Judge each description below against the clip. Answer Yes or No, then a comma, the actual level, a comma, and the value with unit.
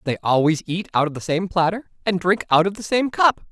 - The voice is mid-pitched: Yes, medium, 180 Hz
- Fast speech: Yes, fast, 255 wpm